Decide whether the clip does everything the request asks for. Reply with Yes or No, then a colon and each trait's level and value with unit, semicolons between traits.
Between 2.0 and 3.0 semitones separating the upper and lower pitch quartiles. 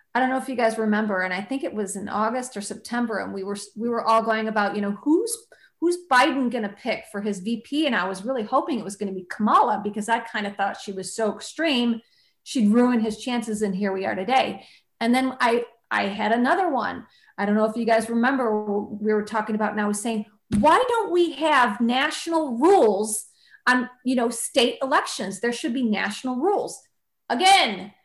No: average, 3.7 semitones